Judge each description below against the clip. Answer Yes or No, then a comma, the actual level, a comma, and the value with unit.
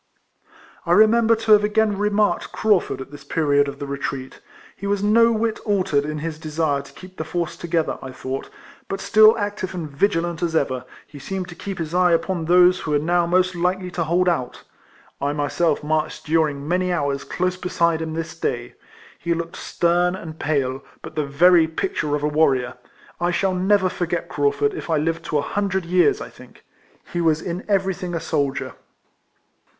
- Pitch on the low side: No, medium, 170 Hz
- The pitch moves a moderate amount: Yes, average, 3.7 semitones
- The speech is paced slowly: No, average, 190 wpm